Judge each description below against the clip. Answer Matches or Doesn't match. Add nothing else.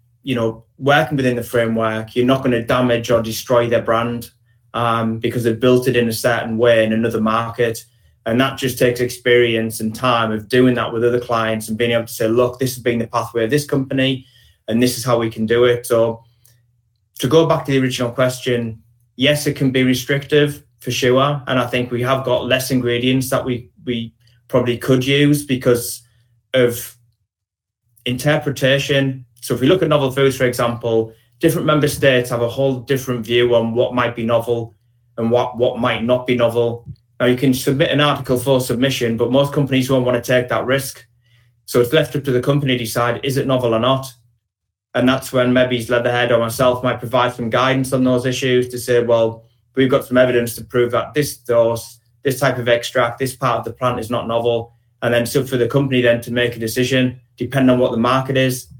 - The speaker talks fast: Matches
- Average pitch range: Doesn't match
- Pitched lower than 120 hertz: Doesn't match